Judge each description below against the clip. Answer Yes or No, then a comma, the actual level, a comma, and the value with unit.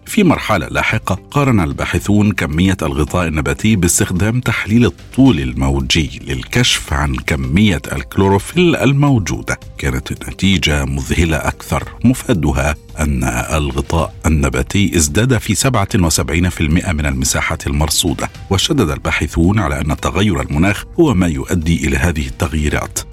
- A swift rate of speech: No, average, 110 wpm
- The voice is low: Yes, very low, 85 Hz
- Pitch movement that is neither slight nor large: No, wide, 5.9 semitones